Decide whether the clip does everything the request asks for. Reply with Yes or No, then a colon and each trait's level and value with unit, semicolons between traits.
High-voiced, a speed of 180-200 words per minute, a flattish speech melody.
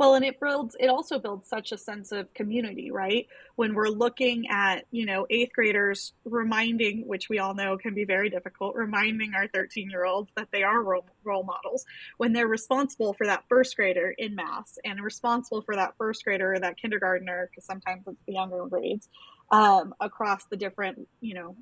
No: high, 210 Hz; average, 195 wpm; average, 3.4 semitones